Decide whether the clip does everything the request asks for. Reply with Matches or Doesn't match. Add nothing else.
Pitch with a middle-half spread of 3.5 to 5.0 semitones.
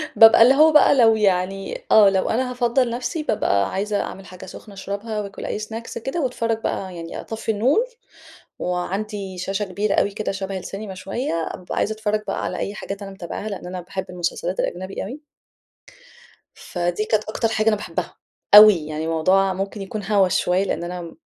Doesn't match